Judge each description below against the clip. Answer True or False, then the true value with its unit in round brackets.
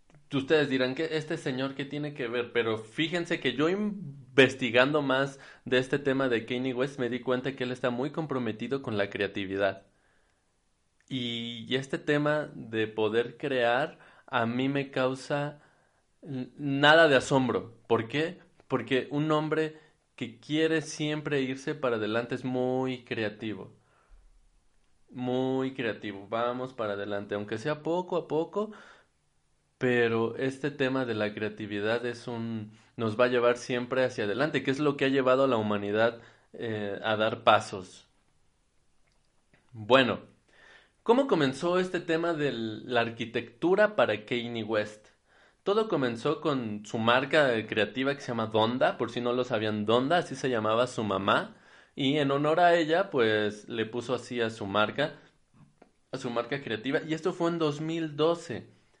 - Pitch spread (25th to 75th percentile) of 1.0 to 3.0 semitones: False (4.4 semitones)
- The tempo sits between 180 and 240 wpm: False (155 wpm)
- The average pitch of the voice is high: False (130 Hz)